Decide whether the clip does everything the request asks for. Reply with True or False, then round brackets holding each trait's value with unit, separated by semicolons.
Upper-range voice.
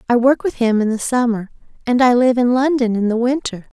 True (240 Hz)